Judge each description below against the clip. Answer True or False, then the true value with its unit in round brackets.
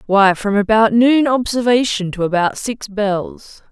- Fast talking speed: False (145 wpm)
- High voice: True (215 Hz)